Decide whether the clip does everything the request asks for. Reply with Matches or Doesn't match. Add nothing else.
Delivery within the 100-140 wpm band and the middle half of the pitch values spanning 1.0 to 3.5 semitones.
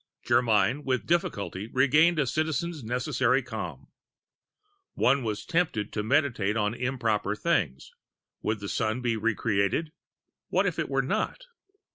Doesn't match